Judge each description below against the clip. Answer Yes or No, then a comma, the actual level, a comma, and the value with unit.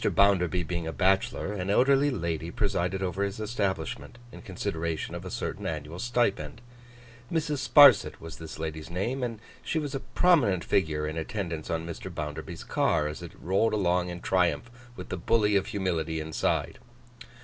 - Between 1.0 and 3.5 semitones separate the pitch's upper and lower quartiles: No, average, 4.8 semitones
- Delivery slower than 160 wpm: No, average, 165 wpm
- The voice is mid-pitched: No, very low, 95 Hz